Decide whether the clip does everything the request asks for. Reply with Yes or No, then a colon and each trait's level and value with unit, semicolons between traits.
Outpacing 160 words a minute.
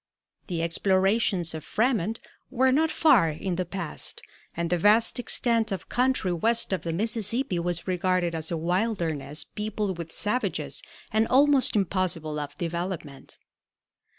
No: average, 140 wpm